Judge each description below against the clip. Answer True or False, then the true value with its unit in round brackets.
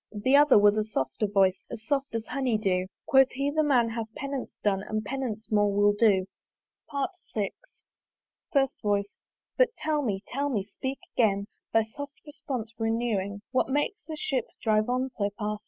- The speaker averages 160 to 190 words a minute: True (170 wpm)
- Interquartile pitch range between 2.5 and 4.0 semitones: False (4.8 semitones)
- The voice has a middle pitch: False (225 Hz)